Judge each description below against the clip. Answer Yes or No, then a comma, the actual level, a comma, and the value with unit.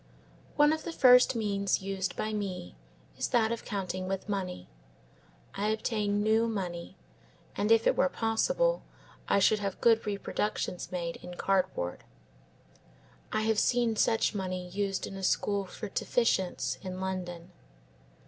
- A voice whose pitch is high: Yes, high, 200 Hz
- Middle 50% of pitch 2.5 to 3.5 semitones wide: Yes, average, 3.2 semitones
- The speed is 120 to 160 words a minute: Yes, average, 145 wpm